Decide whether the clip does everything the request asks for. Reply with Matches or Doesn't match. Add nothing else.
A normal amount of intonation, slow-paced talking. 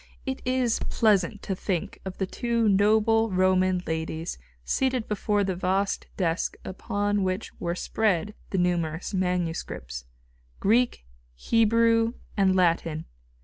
Matches